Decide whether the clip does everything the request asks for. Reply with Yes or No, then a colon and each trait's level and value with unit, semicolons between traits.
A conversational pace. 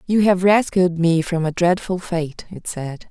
Yes: average, 195 wpm